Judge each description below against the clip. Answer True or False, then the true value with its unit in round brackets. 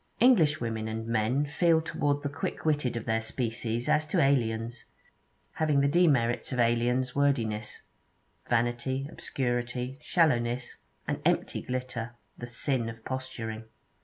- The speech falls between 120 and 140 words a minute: True (135 wpm)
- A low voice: True (125 Hz)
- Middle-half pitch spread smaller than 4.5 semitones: True (3.5 semitones)